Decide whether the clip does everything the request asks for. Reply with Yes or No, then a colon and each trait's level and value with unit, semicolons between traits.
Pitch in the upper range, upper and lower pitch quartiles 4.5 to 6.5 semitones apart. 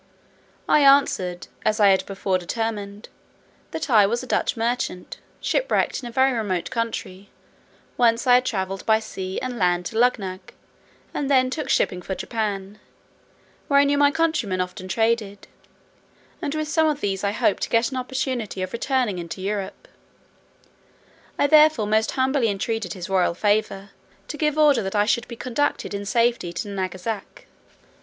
Yes: high, 220 Hz; average, 4.9 semitones